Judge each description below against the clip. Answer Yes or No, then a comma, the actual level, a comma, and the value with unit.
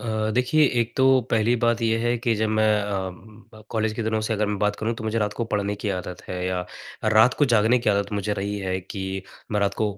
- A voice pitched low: Yes, low, 110 Hz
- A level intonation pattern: Yes, narrow, 2.0 semitones